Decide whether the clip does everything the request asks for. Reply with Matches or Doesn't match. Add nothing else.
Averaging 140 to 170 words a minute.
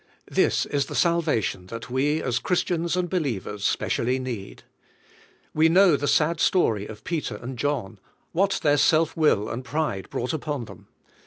Matches